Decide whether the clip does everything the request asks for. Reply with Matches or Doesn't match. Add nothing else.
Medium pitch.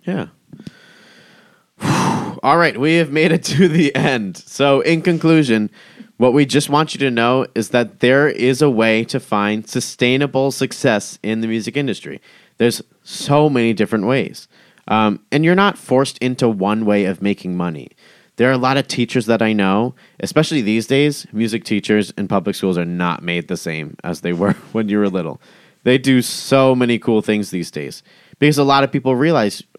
Doesn't match